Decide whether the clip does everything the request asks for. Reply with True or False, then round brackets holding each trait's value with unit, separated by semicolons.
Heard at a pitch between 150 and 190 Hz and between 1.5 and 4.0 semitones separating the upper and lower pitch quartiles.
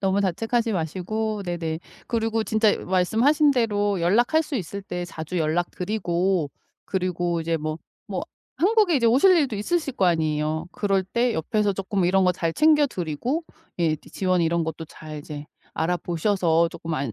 False (185 Hz; 5.2 semitones)